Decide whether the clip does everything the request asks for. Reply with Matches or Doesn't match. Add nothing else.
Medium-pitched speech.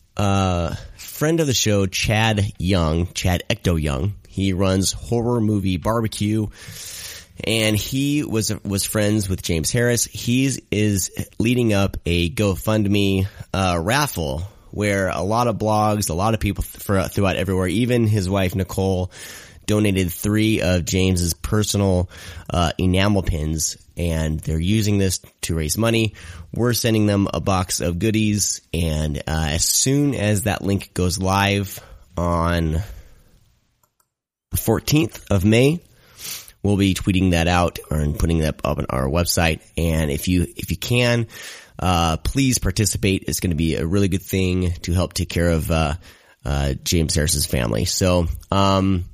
Doesn't match